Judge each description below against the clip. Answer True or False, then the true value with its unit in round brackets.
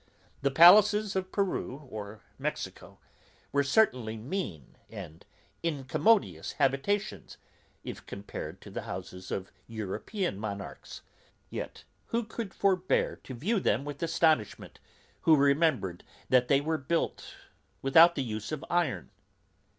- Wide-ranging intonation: True (8.6 semitones)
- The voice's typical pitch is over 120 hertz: True (140 Hz)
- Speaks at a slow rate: True (120 wpm)